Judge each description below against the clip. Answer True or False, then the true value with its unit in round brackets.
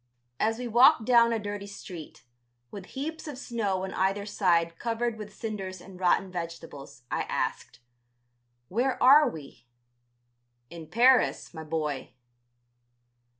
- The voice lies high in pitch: True (200 Hz)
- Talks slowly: True (130 wpm)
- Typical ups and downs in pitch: False (5.8 semitones)